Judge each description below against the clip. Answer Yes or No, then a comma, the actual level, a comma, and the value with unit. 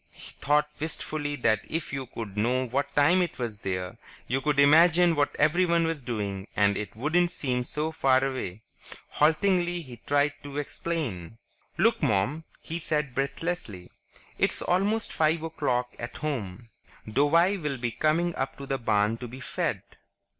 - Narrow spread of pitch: No, wide, 5.4 semitones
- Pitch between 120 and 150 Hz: Yes, medium, 140 Hz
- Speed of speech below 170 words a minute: Yes, average, 160 wpm